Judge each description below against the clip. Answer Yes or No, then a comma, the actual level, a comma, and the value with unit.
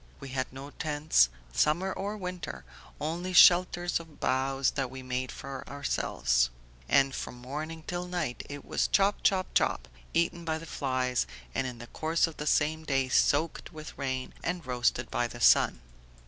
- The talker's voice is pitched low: No, medium, 145 Hz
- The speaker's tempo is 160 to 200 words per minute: Yes, average, 170 wpm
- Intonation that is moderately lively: Yes, average, 4.4 semitones